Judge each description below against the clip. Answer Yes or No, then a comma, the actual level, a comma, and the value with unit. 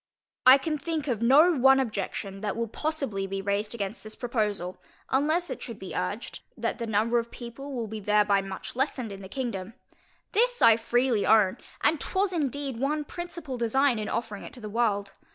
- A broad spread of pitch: No, average, 4.9 semitones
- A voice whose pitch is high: Yes, high, 235 Hz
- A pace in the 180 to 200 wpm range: Yes, average, 190 wpm